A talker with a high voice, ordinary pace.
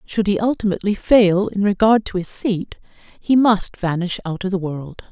Yes: high, 195 Hz; average, 175 wpm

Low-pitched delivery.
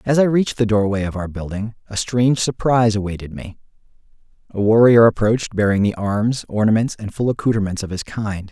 Yes: low, 110 Hz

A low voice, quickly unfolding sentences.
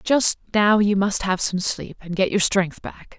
No: high, 195 Hz; fast, 225 wpm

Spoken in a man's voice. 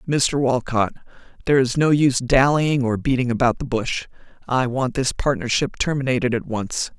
No: female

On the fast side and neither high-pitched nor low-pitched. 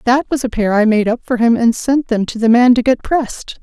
No: fast, 300 wpm; high, 240 Hz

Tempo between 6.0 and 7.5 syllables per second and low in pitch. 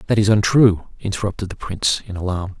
Yes: 6.2 syllables/s; low, 100 Hz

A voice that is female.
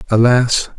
No: male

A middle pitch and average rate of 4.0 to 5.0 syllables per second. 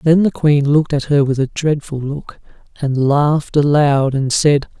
Yes: medium, 145 Hz; 4.5 syllables/s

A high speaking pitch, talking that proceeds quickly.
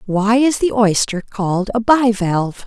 No: high, 215 Hz; average, 180 wpm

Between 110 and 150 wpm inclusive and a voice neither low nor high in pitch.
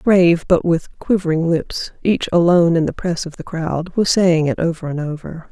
No: fast, 205 wpm; medium, 170 Hz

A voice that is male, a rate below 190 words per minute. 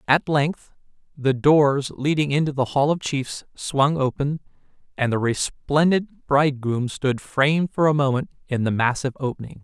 Yes: male; average, 155 wpm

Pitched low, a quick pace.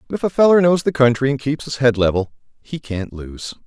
Yes: low, 130 Hz; fast, 245 wpm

